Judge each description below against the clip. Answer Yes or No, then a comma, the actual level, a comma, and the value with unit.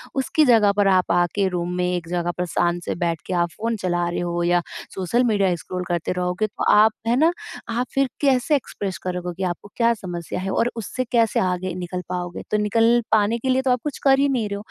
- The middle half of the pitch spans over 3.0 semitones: Yes, average, 4.9 semitones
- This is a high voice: Yes, high, 195 Hz